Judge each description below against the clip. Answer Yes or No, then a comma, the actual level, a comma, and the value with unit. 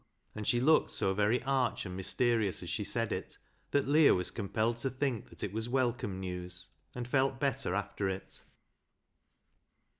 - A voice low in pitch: Yes, low, 115 Hz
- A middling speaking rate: Yes, average, 170 wpm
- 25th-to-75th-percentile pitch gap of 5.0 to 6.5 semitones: Yes, average, 5.3 semitones